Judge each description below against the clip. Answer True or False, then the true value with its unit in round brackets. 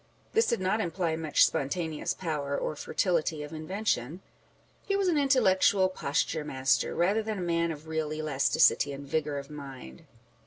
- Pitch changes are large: False (4.3 semitones)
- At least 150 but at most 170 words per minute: True (160 wpm)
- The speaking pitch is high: False (160 Hz)